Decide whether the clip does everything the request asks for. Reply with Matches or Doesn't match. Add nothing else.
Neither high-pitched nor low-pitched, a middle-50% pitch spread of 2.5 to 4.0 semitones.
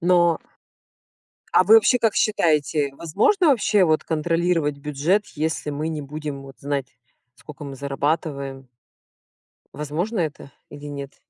Matches